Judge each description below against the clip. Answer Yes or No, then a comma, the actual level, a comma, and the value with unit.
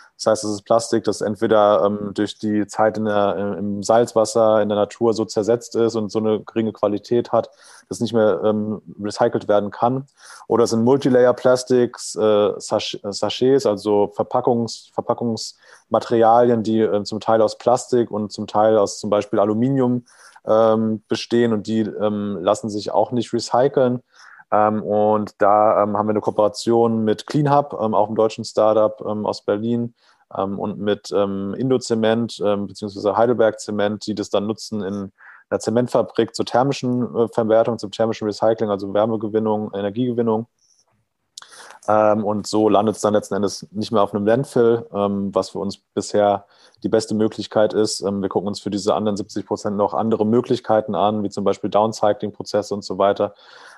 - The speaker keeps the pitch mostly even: Yes, narrow, 1.9 semitones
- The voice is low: Yes, low, 110 Hz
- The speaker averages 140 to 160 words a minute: No, average, 170 wpm